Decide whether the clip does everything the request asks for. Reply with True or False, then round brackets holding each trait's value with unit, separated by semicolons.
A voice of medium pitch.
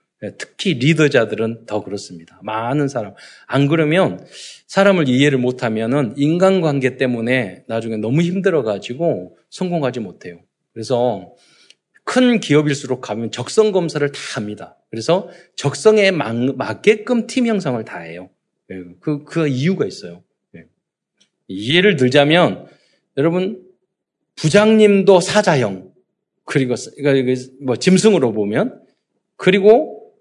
True (145 Hz)